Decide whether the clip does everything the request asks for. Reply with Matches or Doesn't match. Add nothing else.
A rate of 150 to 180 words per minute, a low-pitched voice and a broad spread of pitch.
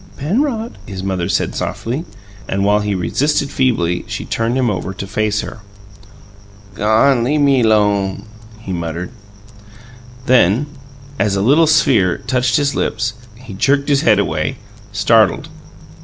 Doesn't match